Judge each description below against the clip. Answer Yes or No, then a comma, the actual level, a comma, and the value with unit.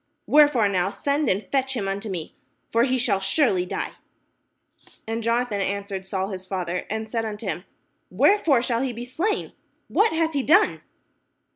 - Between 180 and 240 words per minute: No, average, 165 wpm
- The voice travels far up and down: Yes, wide, 5.7 semitones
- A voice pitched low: No, high, 230 Hz